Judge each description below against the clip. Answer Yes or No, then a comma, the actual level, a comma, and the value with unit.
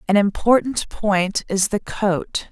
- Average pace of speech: Yes, average, 145 wpm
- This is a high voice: Yes, high, 205 Hz